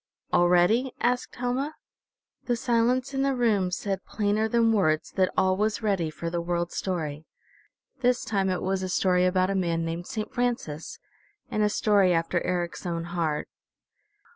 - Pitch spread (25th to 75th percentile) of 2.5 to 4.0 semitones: No, average, 4.8 semitones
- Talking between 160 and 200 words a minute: Yes, average, 165 wpm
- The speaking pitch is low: No, high, 190 Hz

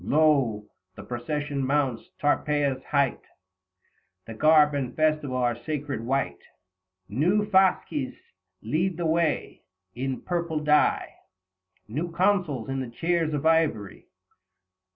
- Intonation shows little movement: No, average, 3.8 semitones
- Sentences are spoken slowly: Yes, slow, 115 wpm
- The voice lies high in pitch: No, medium, 145 Hz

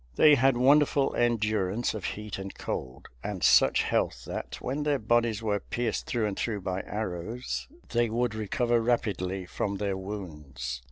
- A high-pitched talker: No, low, 110 Hz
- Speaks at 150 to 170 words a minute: Yes, average, 160 wpm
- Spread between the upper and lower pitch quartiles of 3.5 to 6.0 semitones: Yes, average, 3.8 semitones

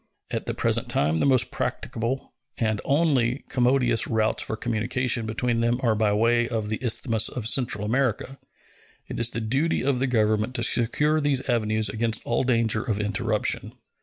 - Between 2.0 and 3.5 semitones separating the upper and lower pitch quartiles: Yes, narrow, 2.6 semitones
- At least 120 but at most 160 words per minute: No, average, 175 wpm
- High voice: No, low, 115 Hz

